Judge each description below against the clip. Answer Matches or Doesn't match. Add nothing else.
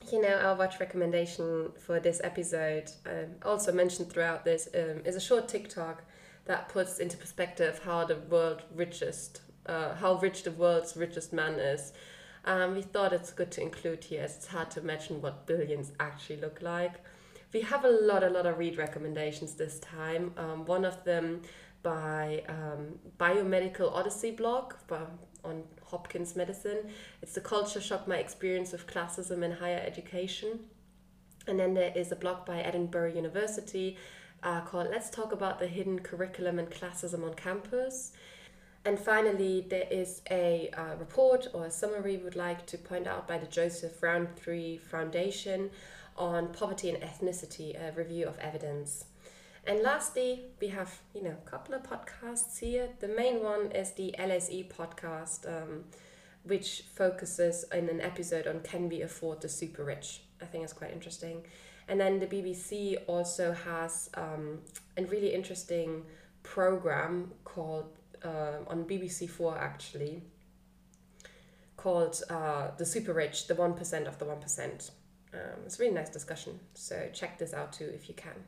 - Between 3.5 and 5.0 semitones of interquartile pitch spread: Doesn't match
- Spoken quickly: Doesn't match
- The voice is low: Doesn't match